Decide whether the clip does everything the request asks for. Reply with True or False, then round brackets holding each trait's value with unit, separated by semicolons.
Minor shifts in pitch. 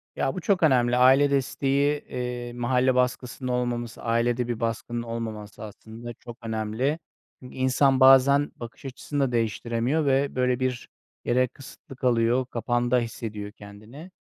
True (2.2 semitones)